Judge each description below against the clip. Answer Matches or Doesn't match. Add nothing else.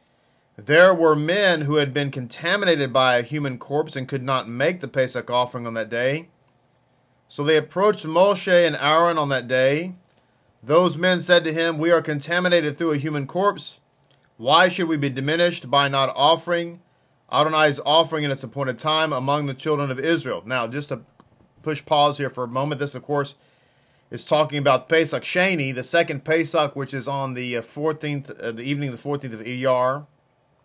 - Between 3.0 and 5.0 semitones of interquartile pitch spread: Matches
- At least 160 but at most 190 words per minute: Matches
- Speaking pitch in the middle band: Matches